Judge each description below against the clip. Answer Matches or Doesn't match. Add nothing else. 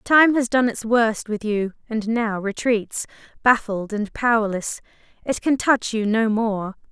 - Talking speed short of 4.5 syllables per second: Matches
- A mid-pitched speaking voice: Doesn't match